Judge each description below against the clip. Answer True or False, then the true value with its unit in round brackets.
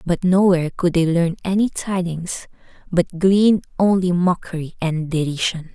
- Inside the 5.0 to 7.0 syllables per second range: False (4.7 syllables/s)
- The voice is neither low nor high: True (175 Hz)